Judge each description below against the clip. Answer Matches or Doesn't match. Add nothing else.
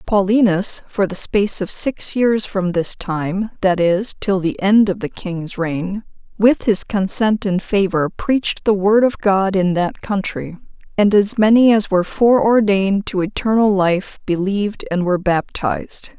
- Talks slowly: Doesn't match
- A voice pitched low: Doesn't match